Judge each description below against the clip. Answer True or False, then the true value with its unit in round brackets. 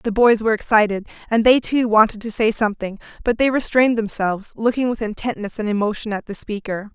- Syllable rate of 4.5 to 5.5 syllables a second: False (6.1 syllables/s)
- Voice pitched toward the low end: False (220 Hz)